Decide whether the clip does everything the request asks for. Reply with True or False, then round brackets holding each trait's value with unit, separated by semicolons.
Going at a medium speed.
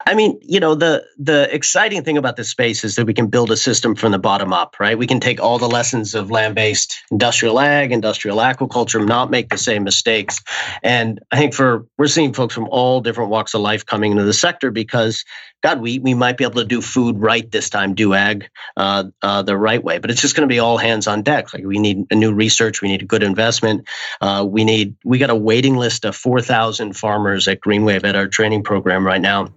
False (240 wpm)